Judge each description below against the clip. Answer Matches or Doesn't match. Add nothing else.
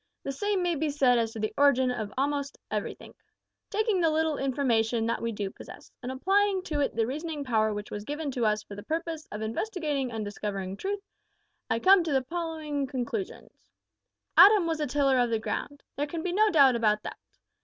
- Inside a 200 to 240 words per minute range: Matches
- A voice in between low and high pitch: Doesn't match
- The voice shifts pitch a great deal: Matches